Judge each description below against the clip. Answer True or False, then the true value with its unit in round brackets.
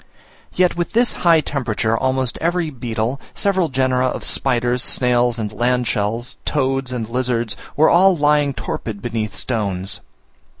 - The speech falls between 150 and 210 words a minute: False (140 wpm)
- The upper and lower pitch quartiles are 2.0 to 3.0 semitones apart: False (4.2 semitones)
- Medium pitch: False (125 Hz)